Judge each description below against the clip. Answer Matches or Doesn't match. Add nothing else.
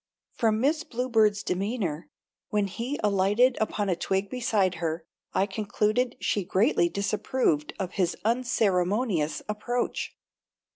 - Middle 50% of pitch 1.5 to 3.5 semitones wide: Doesn't match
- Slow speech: Matches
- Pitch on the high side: Matches